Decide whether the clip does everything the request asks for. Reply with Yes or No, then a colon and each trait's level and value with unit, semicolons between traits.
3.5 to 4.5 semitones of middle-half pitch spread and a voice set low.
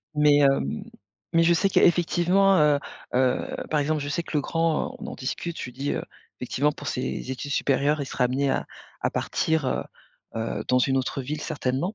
No: average, 3.8 semitones; medium, 145 Hz